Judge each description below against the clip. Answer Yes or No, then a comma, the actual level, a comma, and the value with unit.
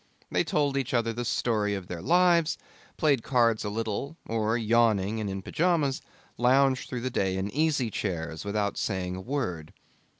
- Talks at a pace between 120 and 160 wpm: No, average, 170 wpm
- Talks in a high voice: No, low, 115 Hz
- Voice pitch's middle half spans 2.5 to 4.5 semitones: No, average, 5.2 semitones